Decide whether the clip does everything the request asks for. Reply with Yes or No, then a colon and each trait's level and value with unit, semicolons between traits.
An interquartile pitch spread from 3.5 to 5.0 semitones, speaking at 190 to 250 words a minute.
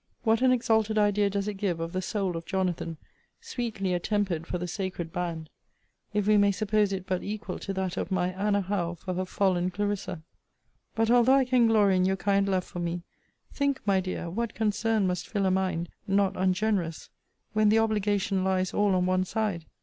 No: narrow, 2.6 semitones; average, 195 wpm